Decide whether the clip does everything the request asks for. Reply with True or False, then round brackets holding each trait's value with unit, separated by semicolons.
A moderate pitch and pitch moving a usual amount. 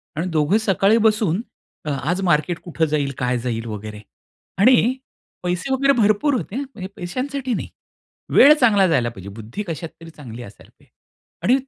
False (180 Hz; 8.4 semitones)